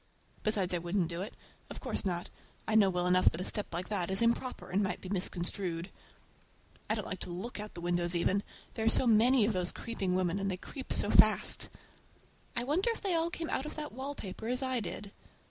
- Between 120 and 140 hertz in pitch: No, high, 200 Hz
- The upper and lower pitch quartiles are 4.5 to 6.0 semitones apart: Yes, average, 4.8 semitones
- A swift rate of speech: Yes, fast, 225 wpm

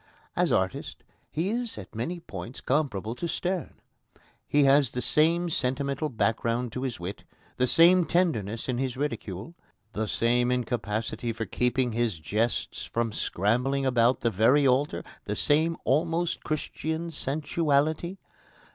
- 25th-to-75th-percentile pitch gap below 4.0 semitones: No, average, 5.2 semitones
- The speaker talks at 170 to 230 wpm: No, average, 140 wpm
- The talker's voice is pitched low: Yes, low, 130 Hz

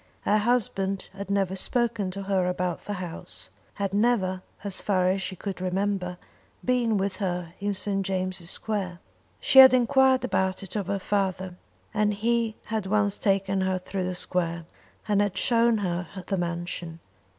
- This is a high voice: Yes, high, 195 Hz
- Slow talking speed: No, average, 165 wpm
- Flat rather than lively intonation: Yes, narrow, 2.2 semitones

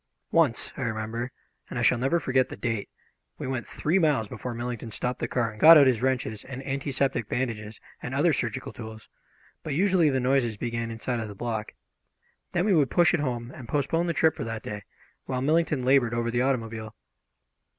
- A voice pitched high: No, low, 125 Hz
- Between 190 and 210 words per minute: Yes, average, 200 wpm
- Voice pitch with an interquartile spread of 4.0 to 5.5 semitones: No, average, 3.4 semitones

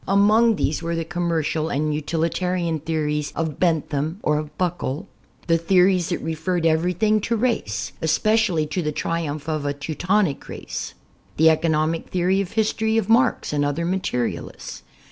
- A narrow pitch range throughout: No, average, 3.4 semitones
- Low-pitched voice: No, medium, 165 Hz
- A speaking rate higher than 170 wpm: No, average, 155 wpm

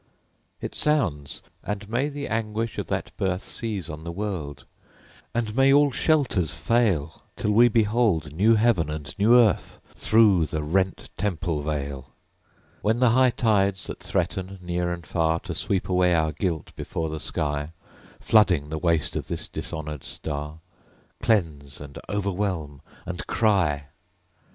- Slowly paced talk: No, average, 145 wpm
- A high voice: No, very low, 90 Hz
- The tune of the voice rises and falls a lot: Yes, wide, 6.0 semitones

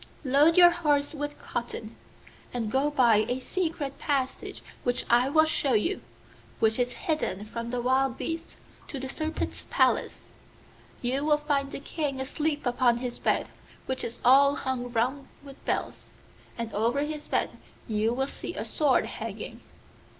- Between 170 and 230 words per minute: No, average, 160 wpm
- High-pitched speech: Yes, very high, 265 Hz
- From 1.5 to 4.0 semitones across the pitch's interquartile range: Yes, average, 3.3 semitones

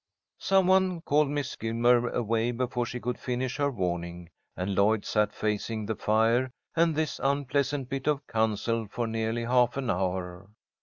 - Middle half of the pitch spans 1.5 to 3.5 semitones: No, average, 4.2 semitones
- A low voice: Yes, low, 120 Hz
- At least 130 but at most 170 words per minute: Yes, average, 160 wpm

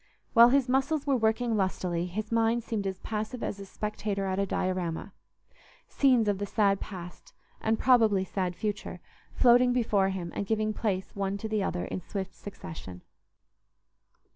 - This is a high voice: Yes, high, 205 Hz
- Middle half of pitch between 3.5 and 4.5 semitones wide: No, average, 3.1 semitones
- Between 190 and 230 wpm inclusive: No, average, 165 wpm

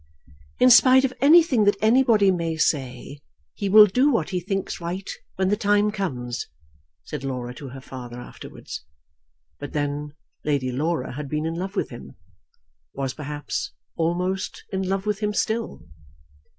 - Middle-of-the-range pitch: Yes, medium, 175 Hz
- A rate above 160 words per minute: No, average, 155 wpm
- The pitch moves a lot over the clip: Yes, wide, 6.5 semitones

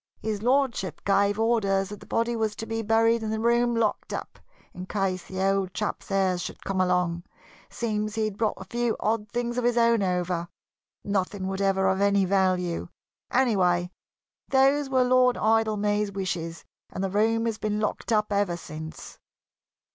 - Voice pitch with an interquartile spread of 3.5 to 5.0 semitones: No, average, 3.1 semitones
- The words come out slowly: No, average, 170 wpm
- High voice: Yes, high, 205 Hz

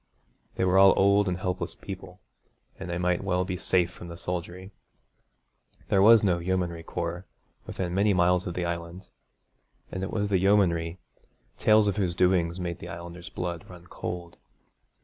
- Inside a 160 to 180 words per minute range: Yes, average, 170 wpm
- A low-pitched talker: Yes, very low, 90 Hz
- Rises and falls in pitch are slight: Yes, narrow, 1.8 semitones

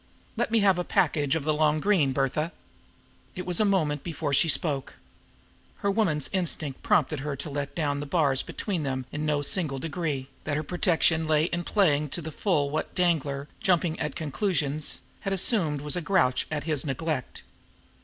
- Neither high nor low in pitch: Yes, medium, 155 Hz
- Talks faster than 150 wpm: Yes, average, 185 wpm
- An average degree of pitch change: Yes, average, 3.5 semitones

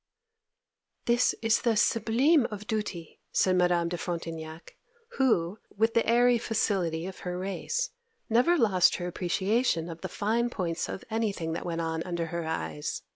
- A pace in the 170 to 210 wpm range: No, average, 155 wpm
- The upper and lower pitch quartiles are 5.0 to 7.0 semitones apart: Yes, average, 5.3 semitones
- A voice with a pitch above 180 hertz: Yes, high, 190 Hz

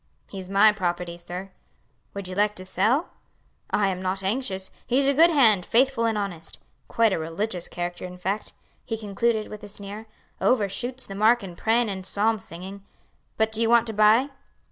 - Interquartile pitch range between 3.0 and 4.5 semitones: Yes, average, 3.3 semitones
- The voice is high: Yes, high, 205 Hz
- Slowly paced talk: No, average, 185 wpm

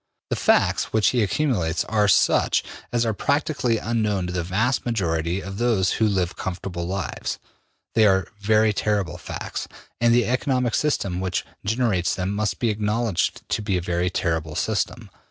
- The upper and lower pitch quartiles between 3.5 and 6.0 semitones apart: Yes, average, 4.2 semitones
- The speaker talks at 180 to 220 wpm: No, average, 165 wpm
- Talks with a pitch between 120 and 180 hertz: No, low, 105 Hz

